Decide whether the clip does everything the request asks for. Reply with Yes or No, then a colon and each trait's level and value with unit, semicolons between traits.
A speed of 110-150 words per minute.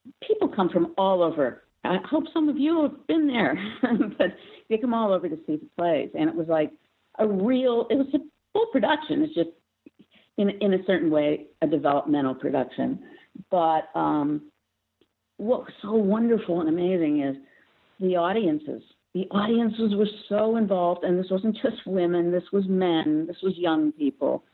No: average, 175 wpm